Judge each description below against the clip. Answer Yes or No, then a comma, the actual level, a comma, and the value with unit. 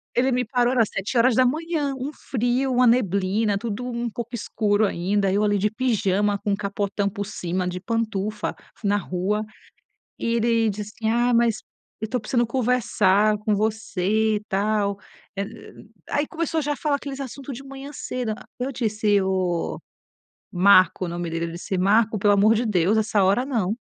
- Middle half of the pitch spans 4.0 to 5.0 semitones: No, average, 3.5 semitones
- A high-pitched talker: Yes, high, 215 Hz